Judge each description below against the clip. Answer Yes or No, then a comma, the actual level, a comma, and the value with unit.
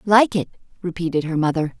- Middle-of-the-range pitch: Yes, medium, 175 Hz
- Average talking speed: Yes, average, 165 wpm